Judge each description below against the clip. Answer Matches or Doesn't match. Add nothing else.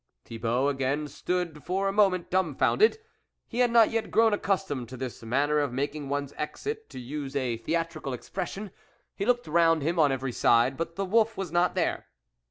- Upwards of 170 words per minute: Matches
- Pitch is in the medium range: Matches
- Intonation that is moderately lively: Doesn't match